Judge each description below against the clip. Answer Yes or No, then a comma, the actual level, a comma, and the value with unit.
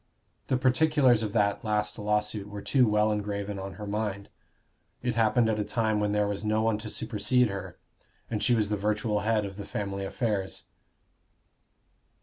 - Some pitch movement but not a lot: No, narrow, 1.6 semitones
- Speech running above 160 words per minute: Yes, average, 175 wpm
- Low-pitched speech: Yes, low, 105 Hz